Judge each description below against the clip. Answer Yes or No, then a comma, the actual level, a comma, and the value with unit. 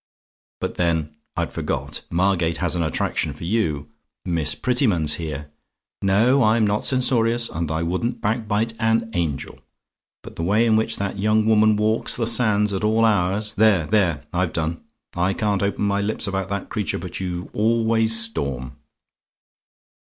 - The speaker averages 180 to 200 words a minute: No, average, 160 wpm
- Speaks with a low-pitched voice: Yes, low, 100 Hz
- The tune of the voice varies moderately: Yes, average, 4.5 semitones